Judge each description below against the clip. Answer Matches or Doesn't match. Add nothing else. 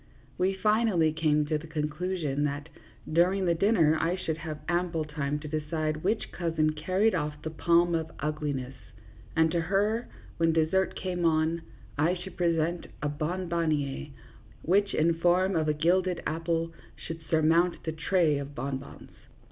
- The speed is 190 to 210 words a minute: Doesn't match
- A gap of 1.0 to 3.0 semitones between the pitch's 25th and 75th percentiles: Matches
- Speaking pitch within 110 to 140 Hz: Doesn't match